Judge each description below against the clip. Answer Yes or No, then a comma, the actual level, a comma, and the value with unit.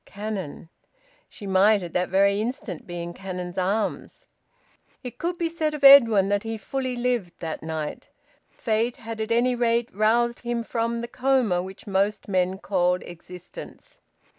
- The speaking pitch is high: Yes, high, 215 Hz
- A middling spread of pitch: Yes, average, 4.4 semitones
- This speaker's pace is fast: No, average, 160 wpm